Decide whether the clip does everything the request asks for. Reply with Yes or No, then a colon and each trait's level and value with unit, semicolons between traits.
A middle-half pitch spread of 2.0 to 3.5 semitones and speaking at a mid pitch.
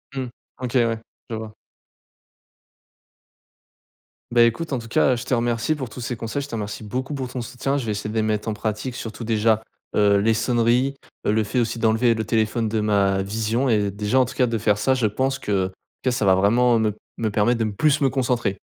No: average, 2.8 semitones; low, 115 Hz